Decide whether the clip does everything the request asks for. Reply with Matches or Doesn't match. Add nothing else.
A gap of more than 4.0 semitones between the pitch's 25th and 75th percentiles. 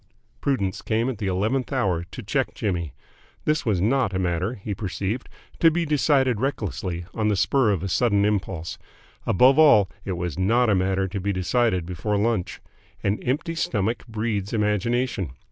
Matches